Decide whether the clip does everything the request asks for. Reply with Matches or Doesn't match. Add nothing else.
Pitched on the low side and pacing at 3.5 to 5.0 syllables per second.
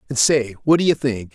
Doesn't match